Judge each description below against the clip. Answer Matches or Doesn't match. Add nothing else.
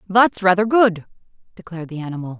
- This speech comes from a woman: Matches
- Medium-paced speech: Matches